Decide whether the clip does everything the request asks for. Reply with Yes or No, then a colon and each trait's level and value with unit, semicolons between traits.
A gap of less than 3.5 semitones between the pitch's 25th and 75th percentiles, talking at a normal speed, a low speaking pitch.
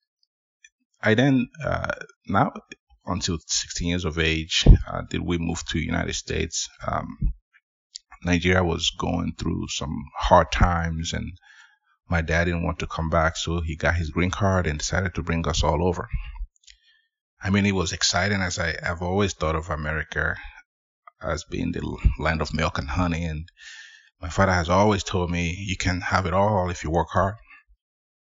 Yes: average, 2.7 semitones; average, 170 wpm; very low, 85 Hz